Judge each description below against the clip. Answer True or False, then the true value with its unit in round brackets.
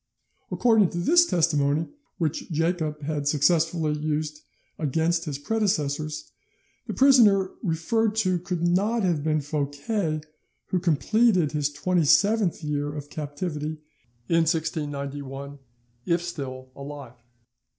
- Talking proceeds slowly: True (115 wpm)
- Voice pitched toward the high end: False (155 Hz)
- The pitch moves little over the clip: False (3.7 semitones)